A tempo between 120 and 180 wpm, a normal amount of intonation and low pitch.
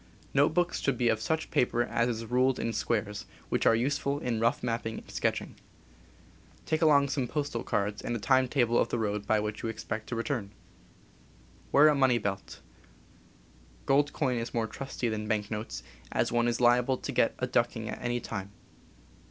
No: average, 190 wpm; average, 3.3 semitones; low, 120 Hz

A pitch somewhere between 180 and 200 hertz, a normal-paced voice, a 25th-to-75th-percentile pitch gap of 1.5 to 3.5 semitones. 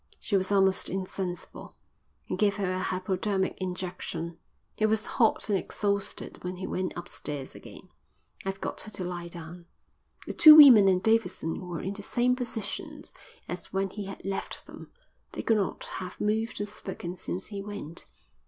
Yes: high, 190 Hz; average, 170 wpm; narrow, 2.5 semitones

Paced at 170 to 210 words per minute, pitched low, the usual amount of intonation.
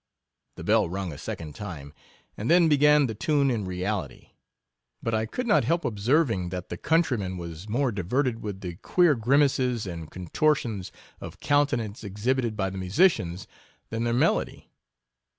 No: average, 175 wpm; low, 110 Hz; wide, 6.9 semitones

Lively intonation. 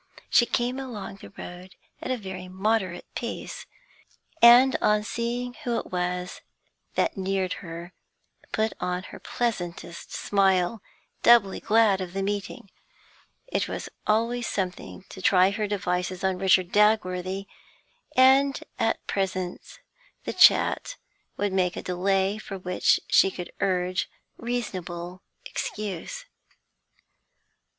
No: average, 3.7 semitones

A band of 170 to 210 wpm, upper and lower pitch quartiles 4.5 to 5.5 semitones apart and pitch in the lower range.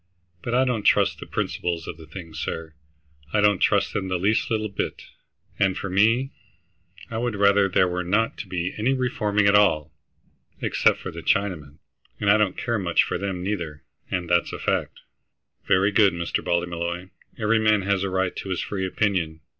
No: average, 190 wpm; average, 3.2 semitones; very low, 95 Hz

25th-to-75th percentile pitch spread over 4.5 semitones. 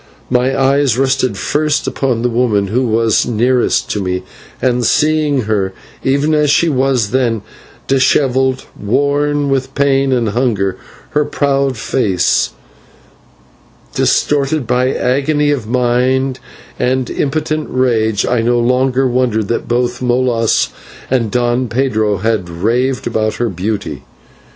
No: average, 3.0 semitones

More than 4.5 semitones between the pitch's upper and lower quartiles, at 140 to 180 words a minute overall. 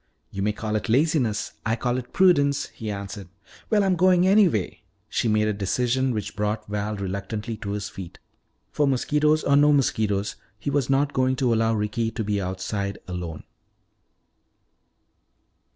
Yes: wide, 5.4 semitones; average, 160 wpm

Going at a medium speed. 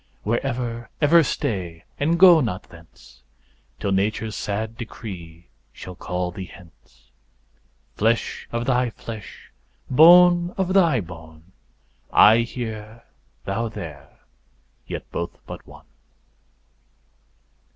No: slow, 110 wpm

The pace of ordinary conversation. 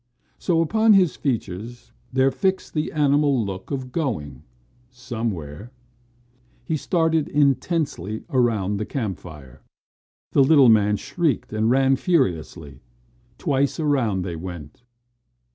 No: slow, 110 wpm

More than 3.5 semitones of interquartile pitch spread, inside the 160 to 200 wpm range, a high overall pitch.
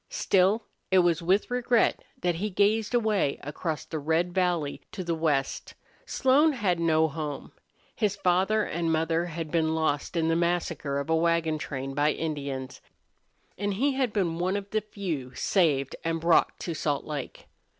No: average, 4.0 semitones; average, 170 wpm; medium, 170 Hz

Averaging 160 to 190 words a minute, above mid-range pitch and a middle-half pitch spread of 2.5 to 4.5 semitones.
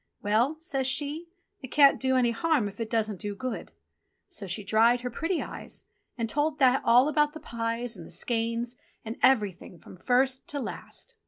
Yes: average, 185 wpm; high, 245 Hz; average, 3.8 semitones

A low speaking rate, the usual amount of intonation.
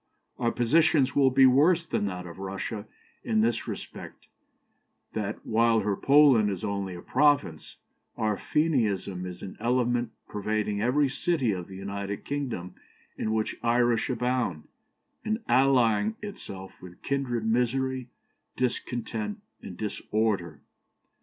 Yes: slow, 125 wpm; average, 4.8 semitones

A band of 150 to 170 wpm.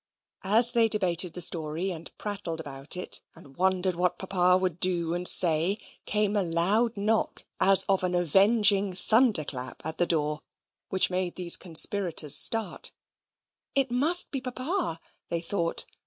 Yes: average, 155 wpm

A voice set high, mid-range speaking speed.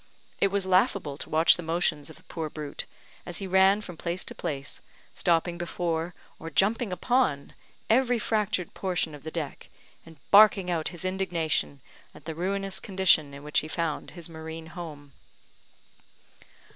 No: medium, 170 Hz; average, 160 wpm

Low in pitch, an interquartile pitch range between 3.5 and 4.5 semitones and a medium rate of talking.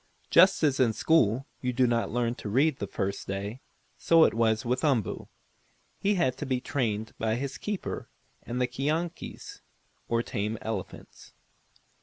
Yes: low, 125 Hz; average, 4.0 semitones; average, 160 wpm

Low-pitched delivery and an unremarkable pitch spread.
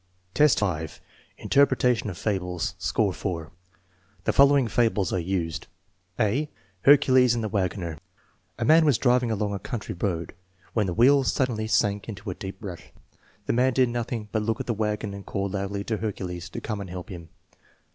Yes: low, 105 Hz; average, 4.3 semitones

